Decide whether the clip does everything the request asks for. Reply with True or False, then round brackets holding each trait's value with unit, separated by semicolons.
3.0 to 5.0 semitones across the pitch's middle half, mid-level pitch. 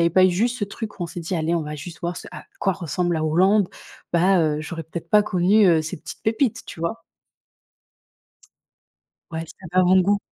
True (3.3 semitones; 175 Hz)